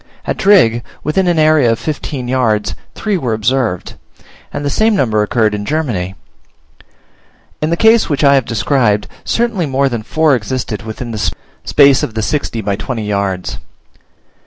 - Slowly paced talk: No, average, 160 wpm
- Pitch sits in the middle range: No, low, 125 Hz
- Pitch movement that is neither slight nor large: No, wide, 6.0 semitones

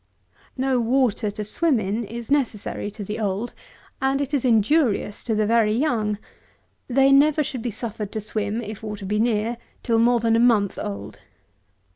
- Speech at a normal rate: Yes, average, 170 wpm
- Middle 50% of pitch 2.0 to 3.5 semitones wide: Yes, average, 2.8 semitones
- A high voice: Yes, high, 225 Hz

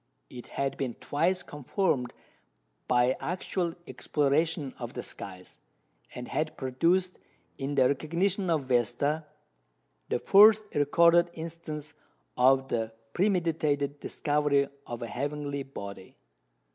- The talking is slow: Yes, slow, 110 wpm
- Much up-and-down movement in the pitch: No, average, 4.3 semitones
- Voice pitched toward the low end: No, medium, 145 Hz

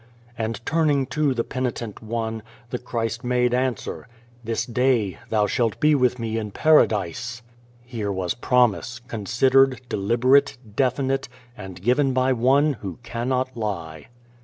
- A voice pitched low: Yes, low, 120 Hz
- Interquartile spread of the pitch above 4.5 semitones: No, average, 2.7 semitones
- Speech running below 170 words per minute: Yes, slow, 135 wpm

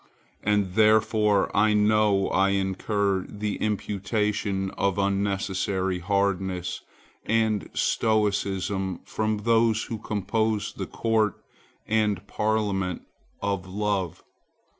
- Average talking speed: No, slow, 95 wpm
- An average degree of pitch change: No, narrow, 1.9 semitones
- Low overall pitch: Yes, low, 100 Hz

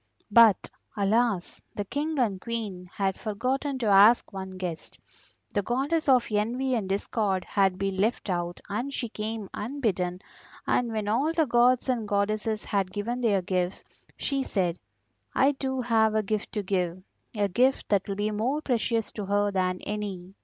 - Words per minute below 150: No, average, 165 wpm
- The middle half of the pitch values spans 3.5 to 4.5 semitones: Yes, average, 3.8 semitones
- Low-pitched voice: No, high, 210 Hz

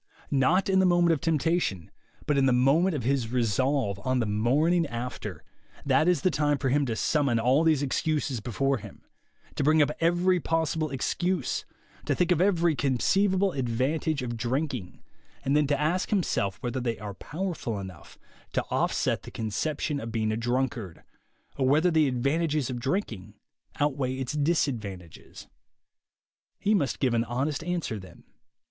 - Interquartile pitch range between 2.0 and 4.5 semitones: No, average, 5.2 semitones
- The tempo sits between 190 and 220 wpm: No, average, 165 wpm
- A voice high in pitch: No, medium, 140 Hz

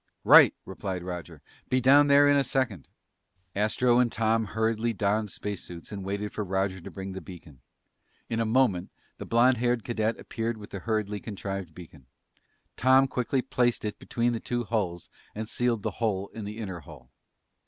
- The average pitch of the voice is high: No, low, 110 Hz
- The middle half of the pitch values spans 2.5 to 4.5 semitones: Yes, average, 3.8 semitones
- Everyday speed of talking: Yes, average, 180 wpm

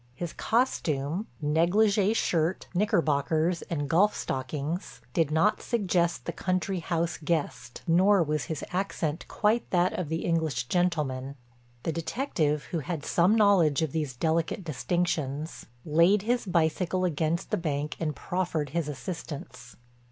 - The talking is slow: Yes, slow, 130 wpm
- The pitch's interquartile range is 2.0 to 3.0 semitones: No, average, 3.4 semitones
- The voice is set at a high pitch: No, medium, 165 Hz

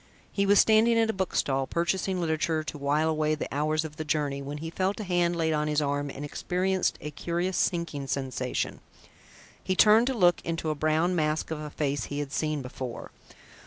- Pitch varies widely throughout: No, average, 3.4 semitones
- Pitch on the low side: No, medium, 155 Hz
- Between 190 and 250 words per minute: Yes, average, 200 wpm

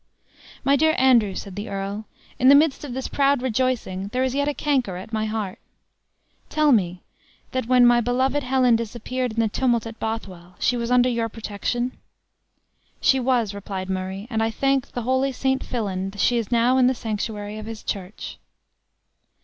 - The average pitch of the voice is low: No, high, 235 Hz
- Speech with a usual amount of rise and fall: Yes, average, 3.8 semitones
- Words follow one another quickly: No, average, 180 wpm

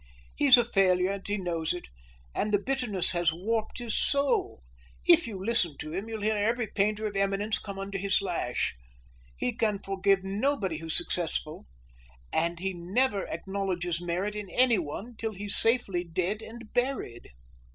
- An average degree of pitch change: Yes, average, 3.8 semitones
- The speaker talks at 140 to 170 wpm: Yes, average, 160 wpm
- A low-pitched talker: No, high, 200 Hz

